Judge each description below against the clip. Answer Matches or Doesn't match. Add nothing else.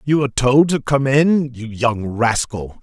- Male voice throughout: Matches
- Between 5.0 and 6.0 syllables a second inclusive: Doesn't match